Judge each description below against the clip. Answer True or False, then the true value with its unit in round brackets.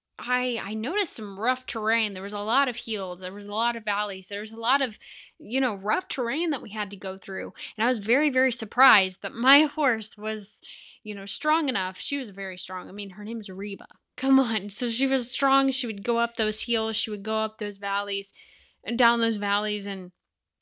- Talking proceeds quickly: True (235 wpm)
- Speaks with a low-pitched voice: False (220 Hz)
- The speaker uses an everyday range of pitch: True (3.8 semitones)